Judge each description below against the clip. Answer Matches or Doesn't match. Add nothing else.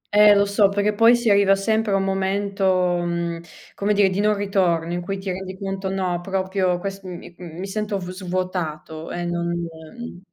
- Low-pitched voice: Doesn't match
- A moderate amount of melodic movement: Doesn't match